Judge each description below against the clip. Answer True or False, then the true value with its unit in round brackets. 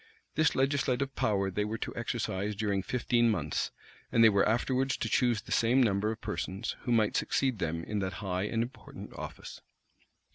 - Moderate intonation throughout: True (3.9 semitones)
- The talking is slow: False (180 wpm)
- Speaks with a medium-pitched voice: False (110 Hz)